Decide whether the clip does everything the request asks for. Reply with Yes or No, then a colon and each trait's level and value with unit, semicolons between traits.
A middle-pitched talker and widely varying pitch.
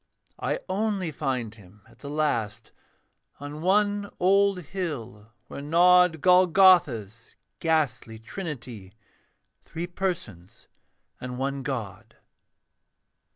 Yes: medium, 150 Hz; wide, 7.8 semitones